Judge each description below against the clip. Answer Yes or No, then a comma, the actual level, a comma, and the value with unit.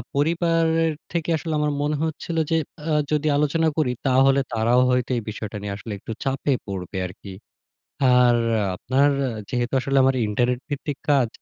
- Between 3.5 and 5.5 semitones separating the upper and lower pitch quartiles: Yes, average, 4.3 semitones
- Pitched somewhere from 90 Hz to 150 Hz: Yes, low, 135 Hz